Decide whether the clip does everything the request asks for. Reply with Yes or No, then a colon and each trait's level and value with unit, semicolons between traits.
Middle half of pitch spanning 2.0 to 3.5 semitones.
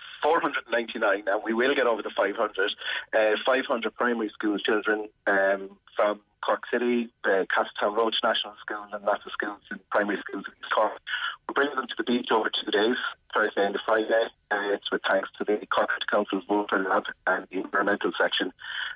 Yes: average, 2.8 semitones